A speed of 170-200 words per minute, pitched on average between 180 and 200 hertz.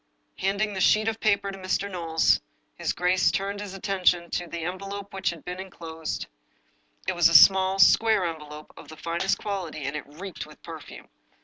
Yes: average, 195 wpm; medium, 185 Hz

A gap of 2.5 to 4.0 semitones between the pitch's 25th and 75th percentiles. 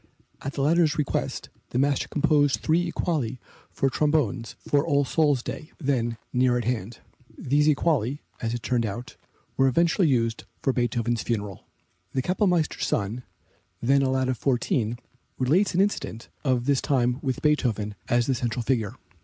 Yes: average, 3.7 semitones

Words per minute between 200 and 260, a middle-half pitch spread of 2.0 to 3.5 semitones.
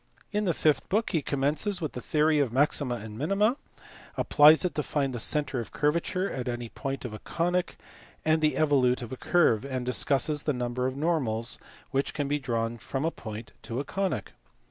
No: fast, 205 wpm; average, 4.3 semitones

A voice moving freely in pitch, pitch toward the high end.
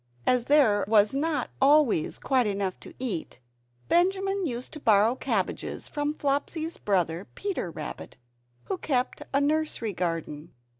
Yes: wide, 7.0 semitones; very high, 255 Hz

